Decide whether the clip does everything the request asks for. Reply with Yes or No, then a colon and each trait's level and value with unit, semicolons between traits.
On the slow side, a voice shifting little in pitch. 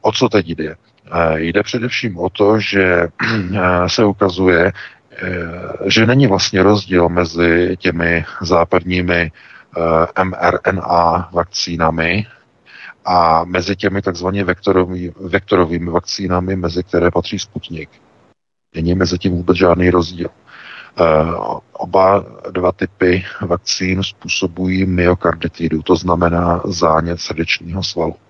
Yes: slow, 100 wpm; narrow, 2.1 semitones